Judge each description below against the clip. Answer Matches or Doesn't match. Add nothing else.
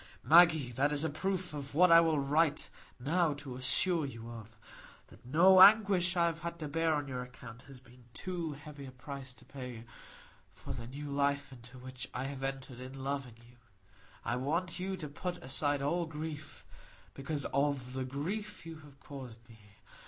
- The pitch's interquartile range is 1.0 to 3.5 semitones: Doesn't match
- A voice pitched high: Doesn't match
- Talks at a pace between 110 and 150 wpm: Doesn't match